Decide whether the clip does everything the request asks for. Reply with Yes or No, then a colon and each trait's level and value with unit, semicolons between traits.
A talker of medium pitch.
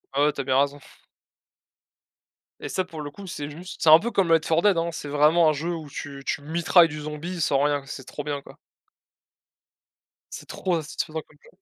Yes: medium, 155 Hz